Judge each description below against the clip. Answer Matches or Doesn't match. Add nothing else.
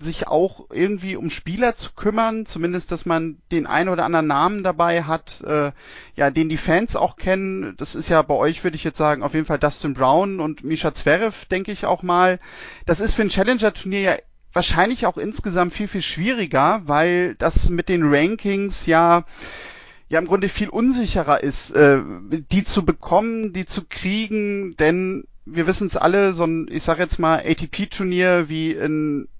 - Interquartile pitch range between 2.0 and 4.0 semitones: Matches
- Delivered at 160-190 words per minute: Matches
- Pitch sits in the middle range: Matches